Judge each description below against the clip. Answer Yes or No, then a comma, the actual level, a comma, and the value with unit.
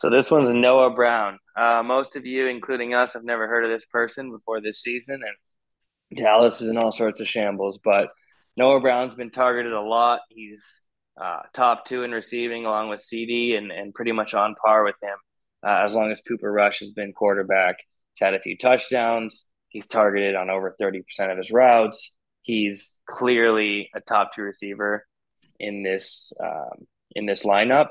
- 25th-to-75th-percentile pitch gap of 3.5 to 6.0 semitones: No, average, 2.9 semitones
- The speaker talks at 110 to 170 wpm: No, average, 185 wpm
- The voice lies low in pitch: Yes, low, 110 Hz